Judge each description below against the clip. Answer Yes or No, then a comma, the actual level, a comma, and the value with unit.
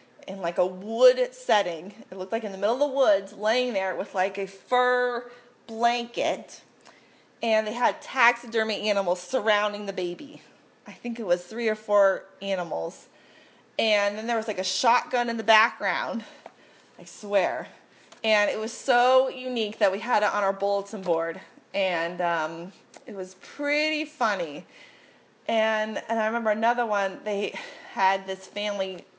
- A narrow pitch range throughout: No, average, 3.6 semitones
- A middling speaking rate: Yes, average, 160 wpm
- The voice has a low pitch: No, high, 215 Hz